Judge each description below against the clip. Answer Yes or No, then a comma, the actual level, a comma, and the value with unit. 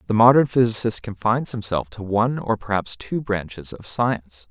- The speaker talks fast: No, average, 175 wpm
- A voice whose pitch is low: Yes, low, 110 Hz